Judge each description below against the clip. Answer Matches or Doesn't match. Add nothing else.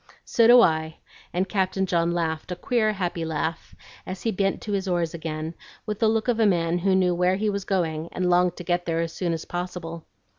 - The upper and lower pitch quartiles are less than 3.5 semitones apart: Matches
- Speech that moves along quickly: Matches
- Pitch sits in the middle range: Matches